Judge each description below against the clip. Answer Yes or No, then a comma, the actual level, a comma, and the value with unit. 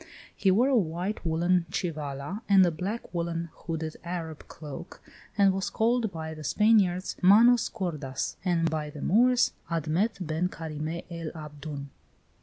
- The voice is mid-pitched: Yes, medium, 170 Hz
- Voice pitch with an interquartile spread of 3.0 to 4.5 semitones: Yes, average, 3.8 semitones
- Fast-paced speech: No, average, 145 wpm